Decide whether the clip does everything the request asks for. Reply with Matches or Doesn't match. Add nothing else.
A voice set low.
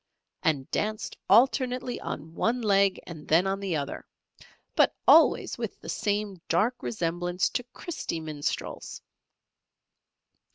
Doesn't match